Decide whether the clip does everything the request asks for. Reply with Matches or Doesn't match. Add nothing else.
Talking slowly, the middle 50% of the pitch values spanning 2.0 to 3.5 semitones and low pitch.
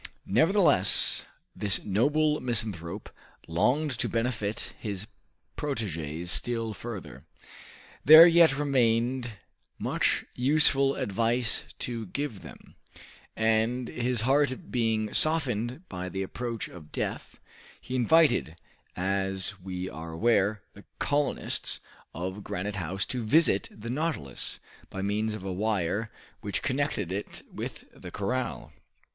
Doesn't match